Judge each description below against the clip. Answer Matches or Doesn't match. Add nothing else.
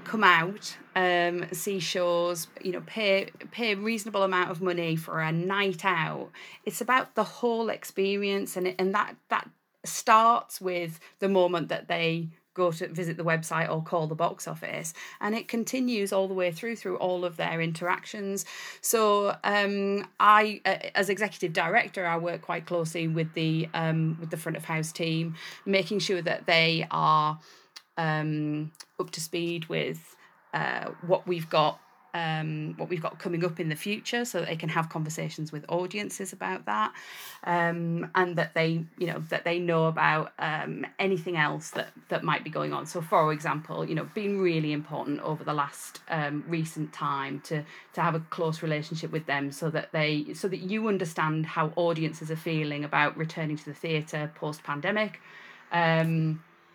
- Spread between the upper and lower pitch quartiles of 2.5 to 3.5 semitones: Matches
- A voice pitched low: Doesn't match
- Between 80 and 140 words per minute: Doesn't match